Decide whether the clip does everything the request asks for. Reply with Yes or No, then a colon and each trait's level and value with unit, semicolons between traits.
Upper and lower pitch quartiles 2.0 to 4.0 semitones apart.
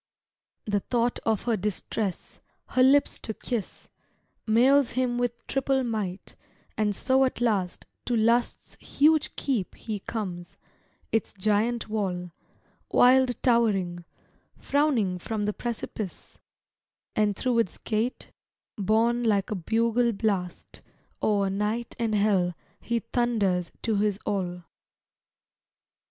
Yes: average, 3.3 semitones